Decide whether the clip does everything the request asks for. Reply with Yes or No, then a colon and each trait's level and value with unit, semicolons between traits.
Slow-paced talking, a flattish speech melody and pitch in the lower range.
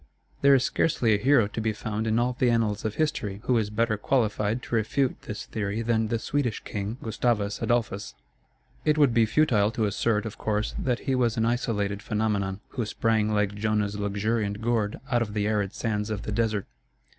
No: average, 195 wpm; narrow, 2.2 semitones; low, 110 Hz